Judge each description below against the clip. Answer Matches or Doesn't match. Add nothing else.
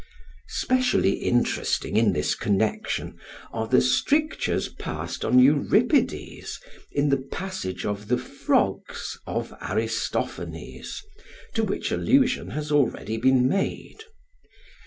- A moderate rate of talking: Doesn't match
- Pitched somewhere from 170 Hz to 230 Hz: Doesn't match